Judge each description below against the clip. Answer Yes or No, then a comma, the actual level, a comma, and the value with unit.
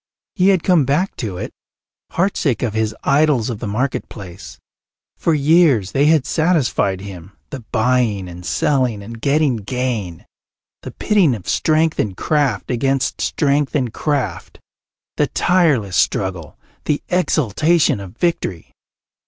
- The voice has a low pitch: Yes, low, 125 Hz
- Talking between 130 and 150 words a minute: Yes, slow, 135 wpm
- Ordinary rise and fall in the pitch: No, wide, 7.2 semitones